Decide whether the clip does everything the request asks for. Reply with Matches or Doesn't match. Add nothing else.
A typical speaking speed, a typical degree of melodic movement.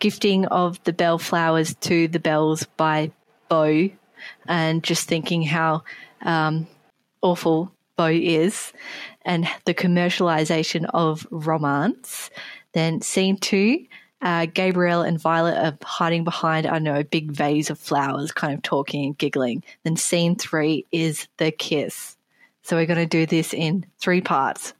Doesn't match